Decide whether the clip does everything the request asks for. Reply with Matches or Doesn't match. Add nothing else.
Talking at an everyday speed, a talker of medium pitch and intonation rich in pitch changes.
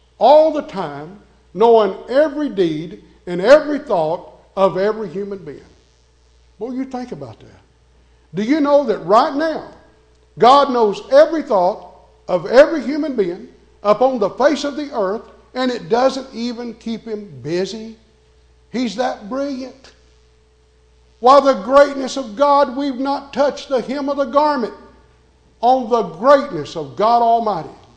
Doesn't match